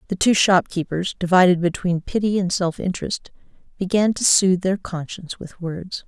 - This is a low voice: No, medium, 185 Hz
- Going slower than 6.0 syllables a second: Yes, 5.2 syllables/s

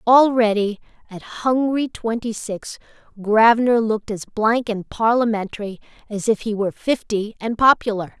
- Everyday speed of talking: No, slow, 130 wpm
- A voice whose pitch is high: Yes, high, 220 Hz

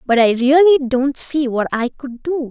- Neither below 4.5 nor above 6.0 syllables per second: Yes, 4.8 syllables/s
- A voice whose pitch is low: No, very high, 265 Hz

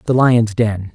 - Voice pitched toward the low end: Yes, low, 110 Hz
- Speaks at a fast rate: No, average, 190 wpm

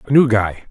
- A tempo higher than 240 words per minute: Yes, fast, 255 wpm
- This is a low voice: Yes, low, 115 Hz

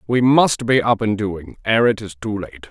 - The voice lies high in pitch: No, low, 110 Hz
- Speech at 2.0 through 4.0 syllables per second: No, 4.8 syllables/s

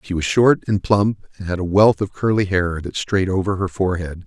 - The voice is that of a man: Yes, male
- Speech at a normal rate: No, fast, 240 wpm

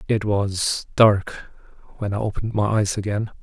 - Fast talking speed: No, average, 160 wpm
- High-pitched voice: No, low, 105 Hz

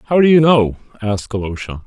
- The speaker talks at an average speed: Yes, average, 195 wpm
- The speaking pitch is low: Yes, low, 120 Hz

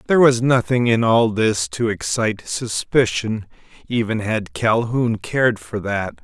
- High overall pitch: No, low, 115 Hz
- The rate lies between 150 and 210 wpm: No, slow, 135 wpm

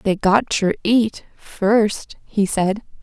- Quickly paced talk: No, slow, 120 wpm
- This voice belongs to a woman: Yes, female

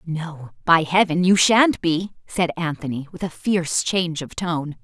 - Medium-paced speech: Yes, average, 175 wpm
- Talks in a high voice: No, medium, 170 Hz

